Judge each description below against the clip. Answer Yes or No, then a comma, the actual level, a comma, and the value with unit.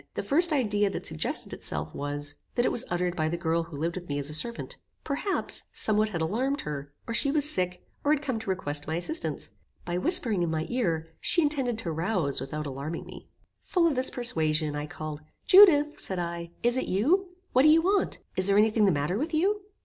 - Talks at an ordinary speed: No, fast, 220 wpm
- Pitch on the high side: Yes, high, 195 Hz